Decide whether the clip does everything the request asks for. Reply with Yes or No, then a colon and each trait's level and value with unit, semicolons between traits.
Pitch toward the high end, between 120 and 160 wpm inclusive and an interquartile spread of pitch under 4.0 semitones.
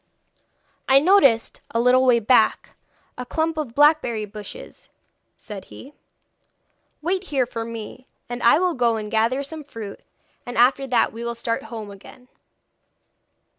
Yes: high, 245 Hz; average, 145 wpm; average, 3.6 semitones